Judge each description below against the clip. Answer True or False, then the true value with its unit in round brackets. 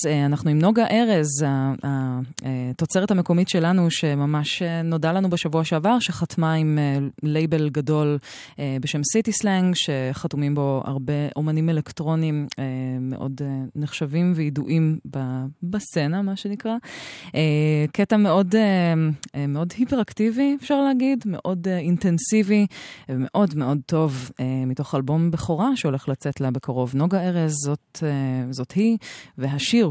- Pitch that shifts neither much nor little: True (4.6 semitones)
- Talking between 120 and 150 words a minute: False (110 wpm)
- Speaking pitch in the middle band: True (155 Hz)